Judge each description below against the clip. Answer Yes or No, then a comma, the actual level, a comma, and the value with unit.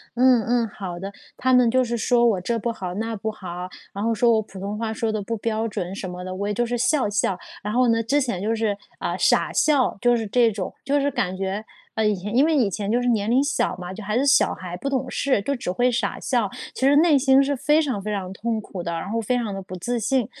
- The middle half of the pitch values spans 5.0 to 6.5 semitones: No, average, 3.9 semitones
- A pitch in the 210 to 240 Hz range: Yes, high, 225 Hz